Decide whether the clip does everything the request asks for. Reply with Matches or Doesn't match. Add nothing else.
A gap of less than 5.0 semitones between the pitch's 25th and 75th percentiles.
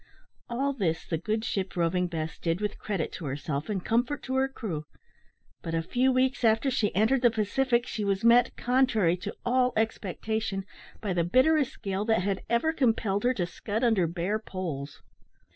Doesn't match